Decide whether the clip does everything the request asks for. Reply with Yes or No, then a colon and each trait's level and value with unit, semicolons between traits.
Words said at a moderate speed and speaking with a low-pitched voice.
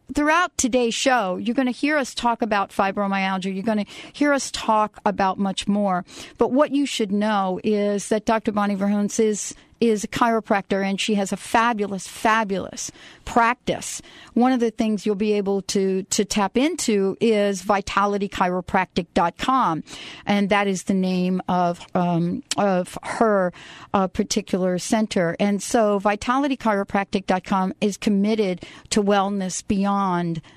No: average, 145 wpm; high, 205 Hz